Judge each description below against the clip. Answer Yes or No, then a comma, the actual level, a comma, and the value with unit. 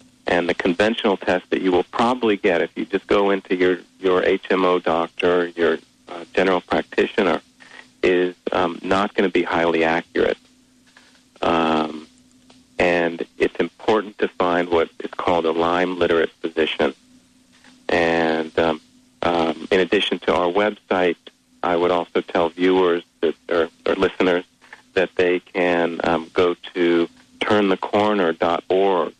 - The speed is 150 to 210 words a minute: No, average, 140 wpm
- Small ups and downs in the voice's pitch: No, average, 3.5 semitones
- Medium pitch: No, very low, 90 Hz